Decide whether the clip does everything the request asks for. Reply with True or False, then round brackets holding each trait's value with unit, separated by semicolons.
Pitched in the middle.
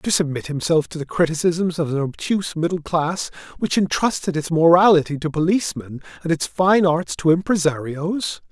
True (165 Hz)